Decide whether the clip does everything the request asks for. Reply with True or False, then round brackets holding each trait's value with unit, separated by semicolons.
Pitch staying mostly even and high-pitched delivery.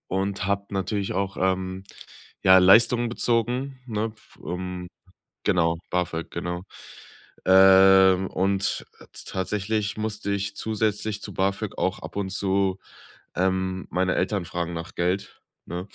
False (1.7 semitones; 95 Hz)